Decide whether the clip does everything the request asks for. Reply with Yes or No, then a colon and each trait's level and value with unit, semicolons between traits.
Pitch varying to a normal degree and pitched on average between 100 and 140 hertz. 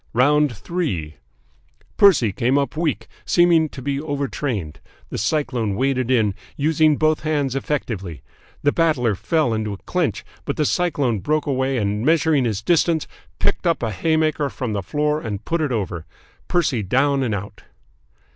No: wide, 5.9 semitones; low, 135 Hz